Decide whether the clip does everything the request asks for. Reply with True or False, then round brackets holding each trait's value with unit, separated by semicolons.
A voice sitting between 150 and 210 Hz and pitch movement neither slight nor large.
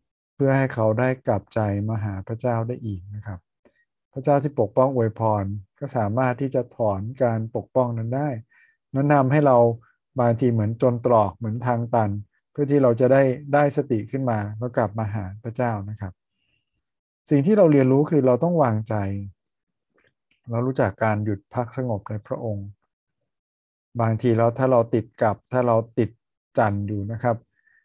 False (120 Hz; 3.4 semitones)